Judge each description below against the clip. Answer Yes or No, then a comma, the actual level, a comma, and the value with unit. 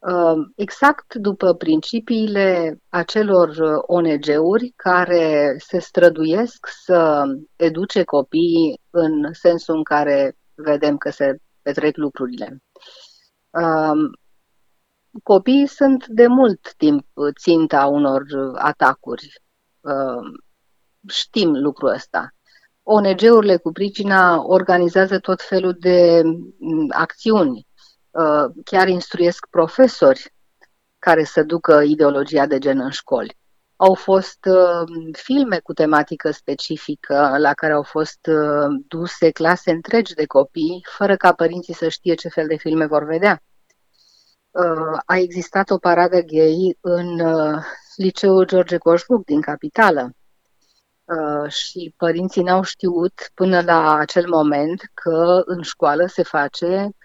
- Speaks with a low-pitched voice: No, medium, 170 Hz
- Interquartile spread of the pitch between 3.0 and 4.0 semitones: Yes, average, 3.6 semitones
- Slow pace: Yes, slow, 110 wpm